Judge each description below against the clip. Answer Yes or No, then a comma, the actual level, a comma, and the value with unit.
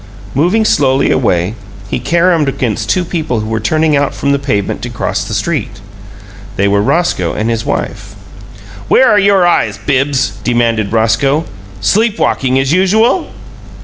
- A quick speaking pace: No, average, 155 wpm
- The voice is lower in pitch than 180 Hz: Yes, low, 135 Hz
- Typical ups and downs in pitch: No, wide, 7.6 semitones